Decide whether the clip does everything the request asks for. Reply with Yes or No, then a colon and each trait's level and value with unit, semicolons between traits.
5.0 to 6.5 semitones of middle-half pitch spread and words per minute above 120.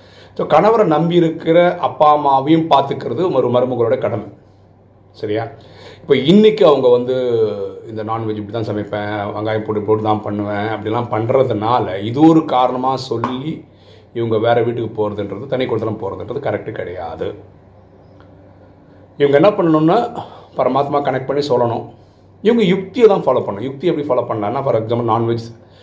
Yes: wide, 5.6 semitones; fast, 130 wpm